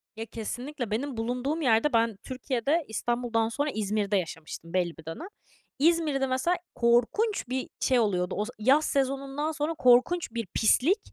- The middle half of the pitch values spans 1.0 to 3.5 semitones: No, average, 4.6 semitones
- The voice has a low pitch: No, high, 245 Hz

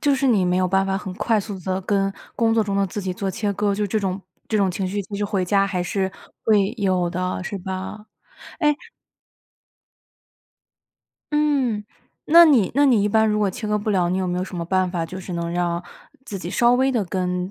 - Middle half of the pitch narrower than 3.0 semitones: Yes, narrow, 2.6 semitones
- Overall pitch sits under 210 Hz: Yes, high, 195 Hz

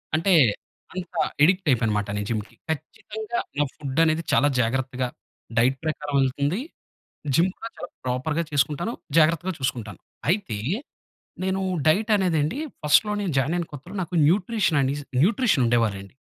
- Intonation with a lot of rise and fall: Yes, wide, 5.9 semitones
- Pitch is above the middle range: No, medium, 155 Hz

